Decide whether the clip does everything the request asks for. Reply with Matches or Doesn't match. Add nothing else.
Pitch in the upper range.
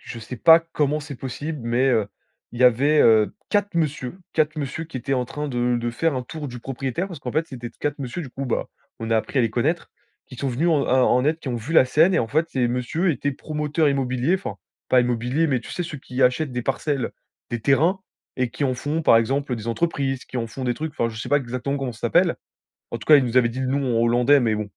Doesn't match